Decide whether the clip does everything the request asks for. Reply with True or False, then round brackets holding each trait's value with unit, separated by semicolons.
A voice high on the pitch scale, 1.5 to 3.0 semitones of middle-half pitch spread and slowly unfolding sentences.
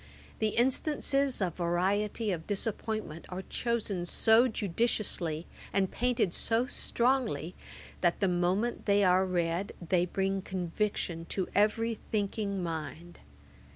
False (195 Hz; 4.1 semitones; 120 wpm)